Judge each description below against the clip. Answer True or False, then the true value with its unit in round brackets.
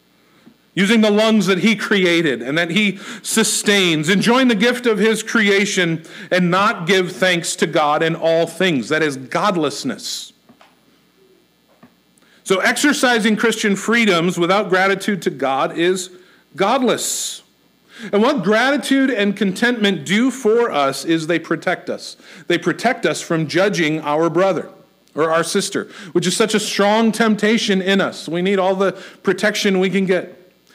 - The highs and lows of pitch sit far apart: False (3.8 semitones)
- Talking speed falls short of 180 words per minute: True (150 wpm)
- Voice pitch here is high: True (195 Hz)